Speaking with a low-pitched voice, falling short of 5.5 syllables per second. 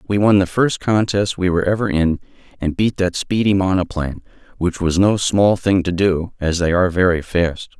Yes: very low, 90 Hz; 5.2 syllables/s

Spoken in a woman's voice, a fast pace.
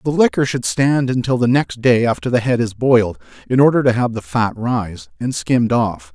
No: male; fast, 225 wpm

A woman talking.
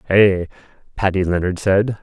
No: male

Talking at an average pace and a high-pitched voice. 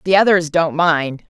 No: average, 175 wpm; medium, 165 Hz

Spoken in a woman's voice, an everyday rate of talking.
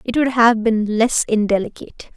Yes: female; average, 165 wpm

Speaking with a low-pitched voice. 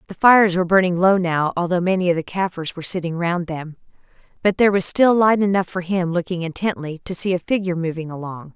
No: medium, 180 Hz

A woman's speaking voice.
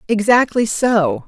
Yes: female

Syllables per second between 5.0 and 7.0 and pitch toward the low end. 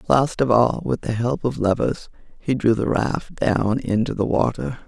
No: 4.4 syllables/s; low, 120 Hz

